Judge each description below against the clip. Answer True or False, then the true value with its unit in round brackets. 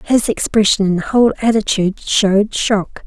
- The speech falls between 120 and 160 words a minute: True (135 wpm)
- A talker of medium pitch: False (210 Hz)